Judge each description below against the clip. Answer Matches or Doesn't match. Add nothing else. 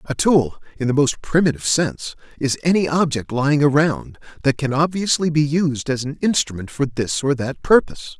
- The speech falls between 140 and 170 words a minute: Doesn't match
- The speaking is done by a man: Matches